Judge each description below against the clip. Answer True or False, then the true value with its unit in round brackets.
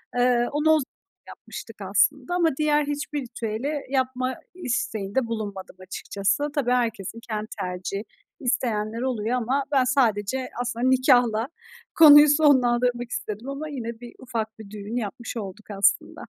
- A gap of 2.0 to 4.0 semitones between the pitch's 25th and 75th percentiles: True (3.6 semitones)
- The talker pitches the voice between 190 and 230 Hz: False (240 Hz)